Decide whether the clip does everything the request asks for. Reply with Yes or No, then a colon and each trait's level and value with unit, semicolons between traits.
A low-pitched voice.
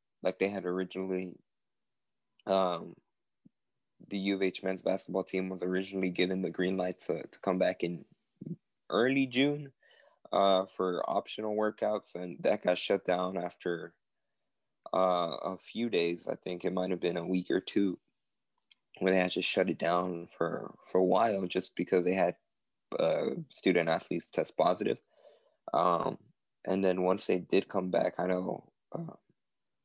Yes: very low, 95 Hz